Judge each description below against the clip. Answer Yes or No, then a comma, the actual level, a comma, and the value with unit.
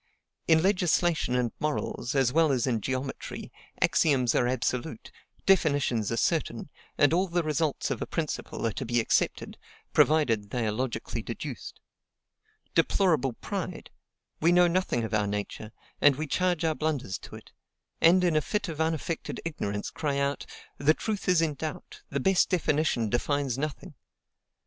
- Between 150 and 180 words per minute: Yes, average, 160 wpm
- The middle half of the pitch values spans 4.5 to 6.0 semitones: Yes, average, 4.9 semitones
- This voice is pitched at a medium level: Yes, medium, 145 Hz